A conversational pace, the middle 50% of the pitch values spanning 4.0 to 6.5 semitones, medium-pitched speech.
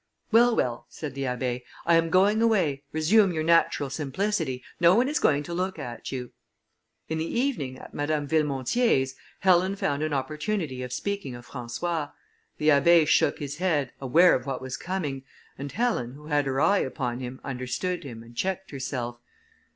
Yes: average, 175 wpm; wide, 5.5 semitones; medium, 150 Hz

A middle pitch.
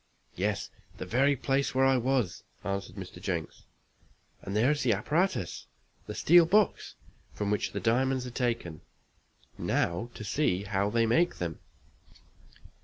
No: low, 115 Hz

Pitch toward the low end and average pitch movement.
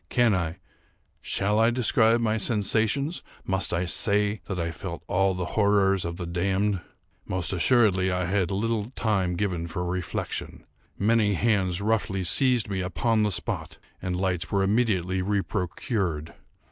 Yes: very low, 95 Hz; average, 3.1 semitones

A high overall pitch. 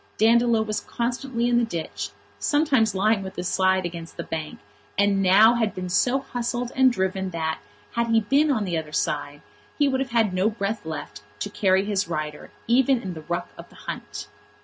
Yes: high, 205 Hz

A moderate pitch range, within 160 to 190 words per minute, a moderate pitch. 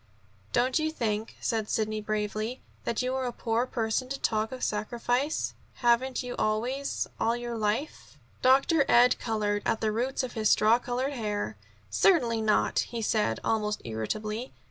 No: average, 3.0 semitones; average, 165 wpm; high, 230 Hz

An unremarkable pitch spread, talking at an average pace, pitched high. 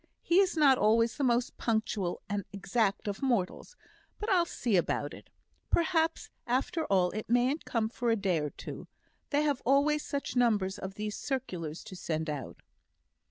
No: wide, 6.2 semitones; average, 170 wpm; high, 230 Hz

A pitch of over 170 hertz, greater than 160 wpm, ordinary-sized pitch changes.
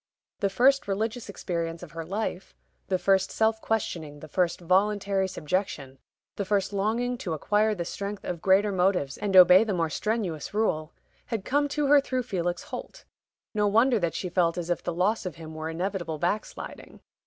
Yes: high, 190 Hz; average, 180 wpm; average, 3.8 semitones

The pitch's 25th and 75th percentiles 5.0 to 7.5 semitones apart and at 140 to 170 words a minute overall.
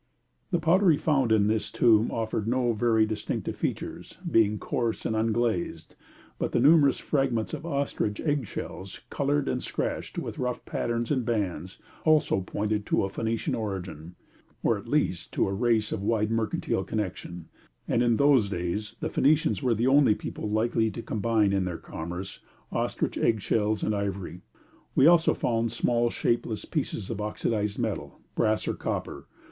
No: average, 3.2 semitones; average, 165 wpm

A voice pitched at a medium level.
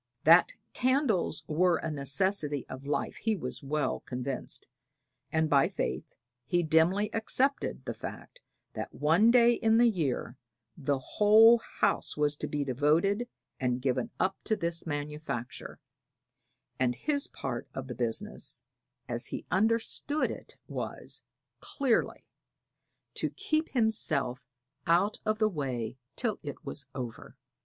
Yes: medium, 160 Hz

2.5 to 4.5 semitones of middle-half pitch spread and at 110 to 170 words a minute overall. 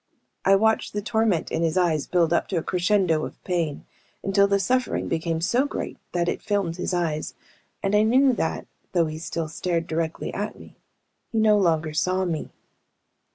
No: average, 3.8 semitones; average, 185 wpm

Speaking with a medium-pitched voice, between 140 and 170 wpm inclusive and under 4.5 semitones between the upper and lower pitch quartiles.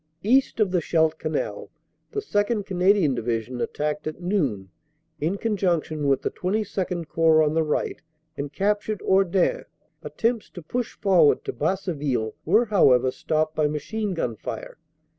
No: medium, 170 Hz; average, 155 wpm; average, 5.3 semitones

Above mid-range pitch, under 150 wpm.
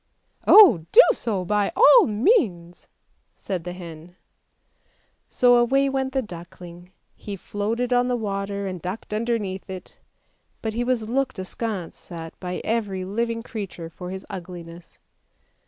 Yes: high, 200 Hz; average, 140 wpm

